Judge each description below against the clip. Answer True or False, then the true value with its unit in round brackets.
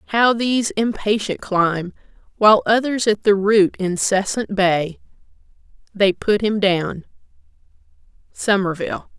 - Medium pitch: False (205 Hz)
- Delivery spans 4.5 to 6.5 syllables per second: False (4.2 syllables/s)